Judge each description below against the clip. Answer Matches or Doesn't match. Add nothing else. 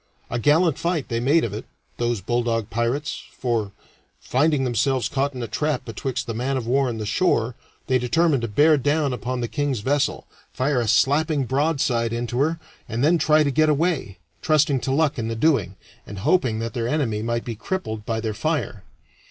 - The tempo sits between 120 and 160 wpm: Doesn't match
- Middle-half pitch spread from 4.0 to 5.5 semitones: Matches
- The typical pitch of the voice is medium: Doesn't match